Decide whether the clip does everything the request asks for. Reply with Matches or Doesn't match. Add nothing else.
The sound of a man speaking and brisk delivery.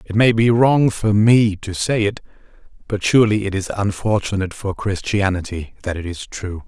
Doesn't match